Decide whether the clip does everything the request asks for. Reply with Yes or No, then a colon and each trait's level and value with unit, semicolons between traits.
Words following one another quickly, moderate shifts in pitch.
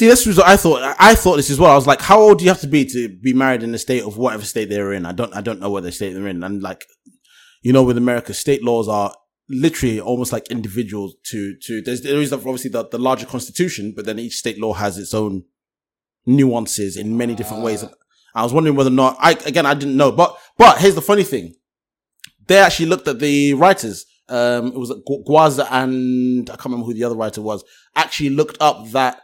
Yes: fast, 245 wpm; average, 4.5 semitones